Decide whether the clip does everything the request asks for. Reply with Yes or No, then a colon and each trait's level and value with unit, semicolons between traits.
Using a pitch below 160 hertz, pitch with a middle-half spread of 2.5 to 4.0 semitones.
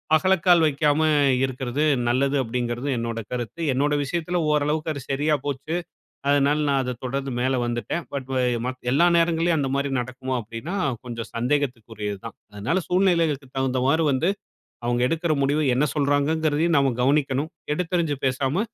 Yes: medium, 140 Hz; average, 3.7 semitones